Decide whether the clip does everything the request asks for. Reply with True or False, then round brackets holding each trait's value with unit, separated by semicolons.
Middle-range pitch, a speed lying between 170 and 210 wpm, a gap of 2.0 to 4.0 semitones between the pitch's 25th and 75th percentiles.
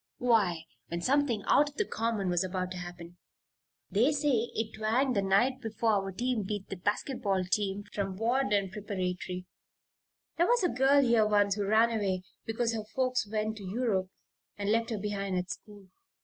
False (210 Hz; 180 wpm; 3.7 semitones)